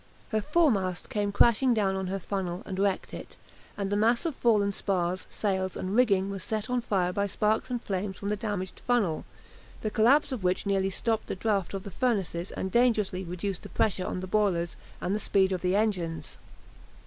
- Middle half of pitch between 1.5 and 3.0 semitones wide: Yes, average, 2.7 semitones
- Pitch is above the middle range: Yes, high, 200 Hz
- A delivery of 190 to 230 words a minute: Yes, average, 200 wpm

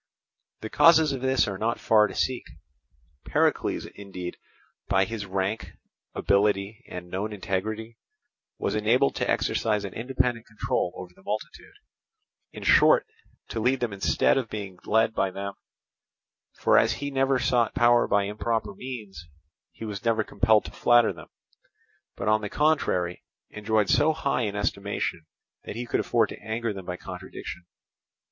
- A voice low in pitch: Yes, low, 110 Hz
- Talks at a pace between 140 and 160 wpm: Yes, average, 155 wpm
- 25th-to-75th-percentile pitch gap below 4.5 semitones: Yes, average, 3.5 semitones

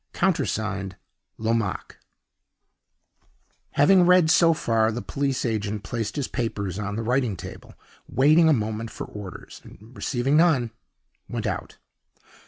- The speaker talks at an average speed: No, slow, 125 wpm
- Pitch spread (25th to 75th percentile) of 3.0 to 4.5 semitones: No, average, 5.3 semitones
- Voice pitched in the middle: No, low, 115 Hz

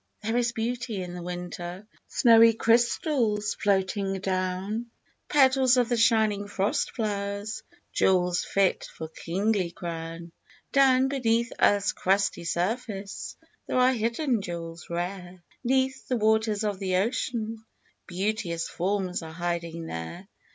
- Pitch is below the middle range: No, high, 205 Hz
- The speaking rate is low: Yes, slow, 125 wpm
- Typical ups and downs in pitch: Yes, average, 4.4 semitones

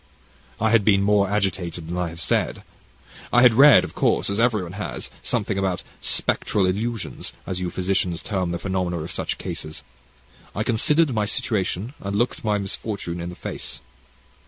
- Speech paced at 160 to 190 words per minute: Yes, average, 170 wpm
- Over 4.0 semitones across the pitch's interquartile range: No, average, 3.5 semitones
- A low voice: Yes, low, 100 Hz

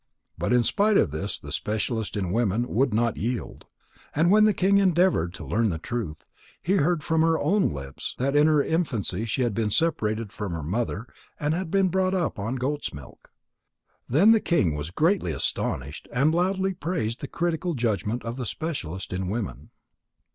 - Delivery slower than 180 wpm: No, average, 185 wpm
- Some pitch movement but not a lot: No, wide, 8.5 semitones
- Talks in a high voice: No, low, 125 Hz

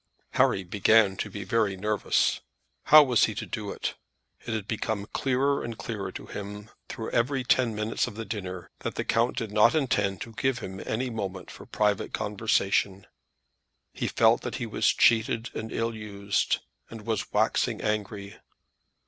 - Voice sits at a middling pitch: No, low, 110 Hz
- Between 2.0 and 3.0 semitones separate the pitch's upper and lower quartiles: Yes, narrow, 2.5 semitones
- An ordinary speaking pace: Yes, average, 170 wpm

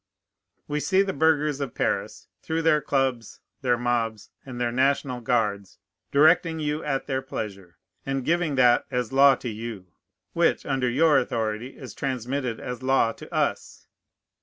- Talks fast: No, average, 155 wpm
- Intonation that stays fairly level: No, average, 3.6 semitones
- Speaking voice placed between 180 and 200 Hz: No, low, 130 Hz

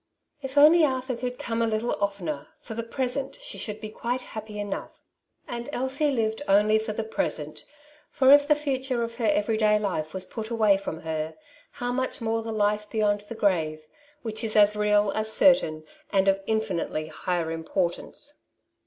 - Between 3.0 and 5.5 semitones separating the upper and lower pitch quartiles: Yes, average, 3.5 semitones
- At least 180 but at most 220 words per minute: Yes, average, 185 wpm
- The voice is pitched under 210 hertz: No, high, 220 Hz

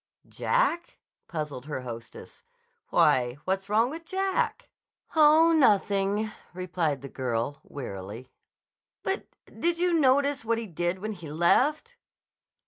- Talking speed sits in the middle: No, slow, 115 wpm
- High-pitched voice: Yes, high, 200 Hz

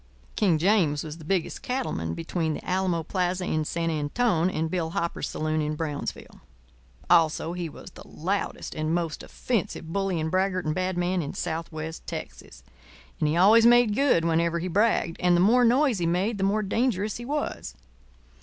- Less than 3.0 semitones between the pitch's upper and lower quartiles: No, average, 3.8 semitones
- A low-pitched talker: No, medium, 175 Hz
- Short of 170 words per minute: No, average, 180 wpm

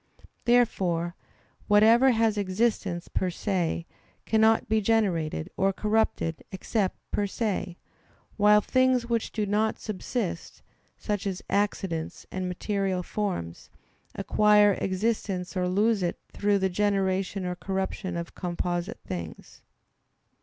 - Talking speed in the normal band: No, slow, 115 wpm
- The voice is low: No, high, 195 Hz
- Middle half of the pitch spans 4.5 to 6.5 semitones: No, average, 2.9 semitones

